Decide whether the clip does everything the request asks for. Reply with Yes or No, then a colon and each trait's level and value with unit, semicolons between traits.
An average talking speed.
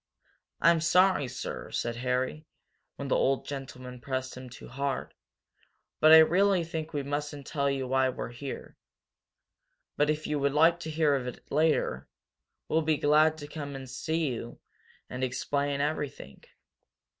Yes: average, 155 wpm